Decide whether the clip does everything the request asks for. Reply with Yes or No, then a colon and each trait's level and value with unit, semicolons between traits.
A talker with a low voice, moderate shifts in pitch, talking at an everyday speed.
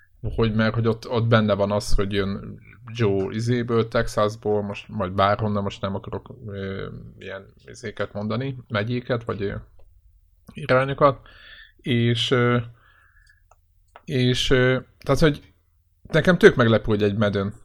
Yes: low, 110 Hz; average, 3.4 semitones; average, 135 wpm